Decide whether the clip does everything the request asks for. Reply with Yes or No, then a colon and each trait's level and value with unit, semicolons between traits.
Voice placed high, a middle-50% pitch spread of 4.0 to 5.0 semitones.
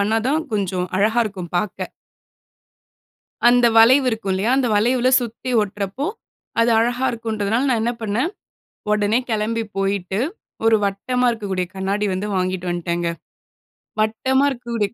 No: high, 215 Hz; average, 3.6 semitones